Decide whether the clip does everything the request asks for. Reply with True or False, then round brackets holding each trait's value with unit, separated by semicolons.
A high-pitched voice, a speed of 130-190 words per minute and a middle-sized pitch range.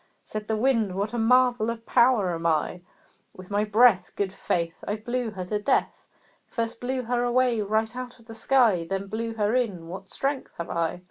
False (220 Hz; 200 wpm; 3.9 semitones)